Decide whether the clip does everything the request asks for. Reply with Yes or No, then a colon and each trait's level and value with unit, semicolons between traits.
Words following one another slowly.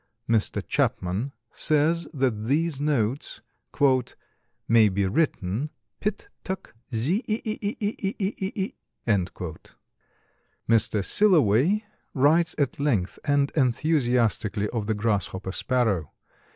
Yes: slow, 110 wpm